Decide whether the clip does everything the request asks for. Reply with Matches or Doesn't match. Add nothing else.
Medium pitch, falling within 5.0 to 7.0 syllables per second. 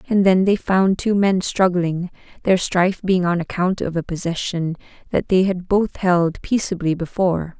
Doesn't match